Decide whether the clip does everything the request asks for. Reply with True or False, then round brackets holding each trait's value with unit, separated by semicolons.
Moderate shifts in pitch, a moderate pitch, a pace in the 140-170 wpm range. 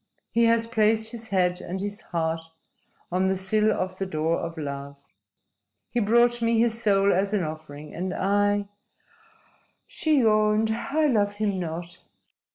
False (3.8 semitones; 205 Hz; 155 wpm)